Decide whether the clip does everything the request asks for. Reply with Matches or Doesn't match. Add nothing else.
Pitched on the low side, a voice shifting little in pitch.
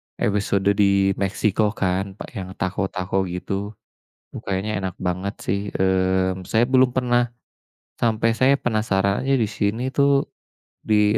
Doesn't match